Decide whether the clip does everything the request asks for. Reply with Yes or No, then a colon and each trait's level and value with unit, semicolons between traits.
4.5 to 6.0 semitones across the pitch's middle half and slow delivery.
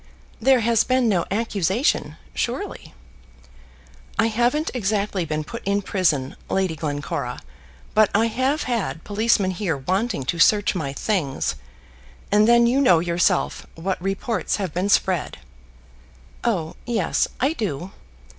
Yes: wide, 5.4 semitones; slow, 130 wpm